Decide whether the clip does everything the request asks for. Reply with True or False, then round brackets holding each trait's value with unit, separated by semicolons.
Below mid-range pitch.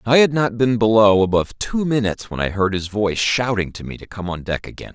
True (105 Hz)